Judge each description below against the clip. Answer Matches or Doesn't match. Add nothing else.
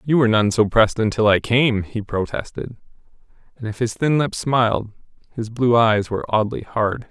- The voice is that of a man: Matches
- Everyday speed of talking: Matches